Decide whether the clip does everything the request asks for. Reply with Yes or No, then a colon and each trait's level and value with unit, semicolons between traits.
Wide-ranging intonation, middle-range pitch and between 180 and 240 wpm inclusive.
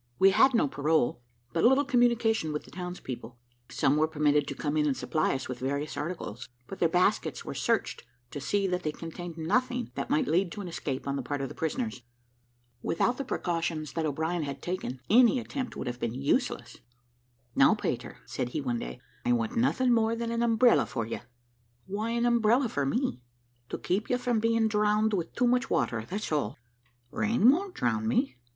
Yes: wide, 8.5 semitones; medium, 180 Hz; average, 200 wpm